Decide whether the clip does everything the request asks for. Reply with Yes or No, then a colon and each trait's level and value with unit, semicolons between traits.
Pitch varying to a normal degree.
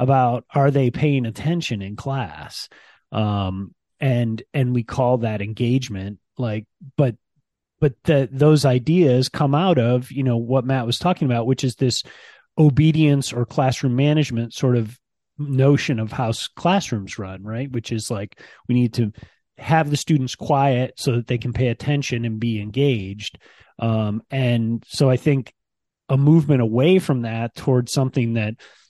Yes: average, 3.5 semitones